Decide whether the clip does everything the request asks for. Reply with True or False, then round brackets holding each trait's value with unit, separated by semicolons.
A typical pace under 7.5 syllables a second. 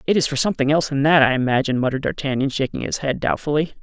False (7.7 syllables/s)